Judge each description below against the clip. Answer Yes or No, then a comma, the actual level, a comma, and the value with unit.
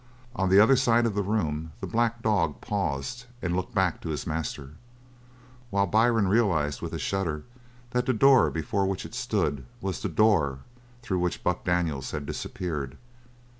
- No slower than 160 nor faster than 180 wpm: Yes, average, 170 wpm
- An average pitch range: No, wide, 5.9 semitones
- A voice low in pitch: Yes, very low, 95 Hz